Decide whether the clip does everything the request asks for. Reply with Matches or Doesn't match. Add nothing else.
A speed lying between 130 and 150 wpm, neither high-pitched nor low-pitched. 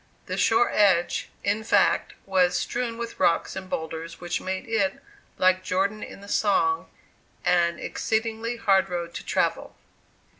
Doesn't match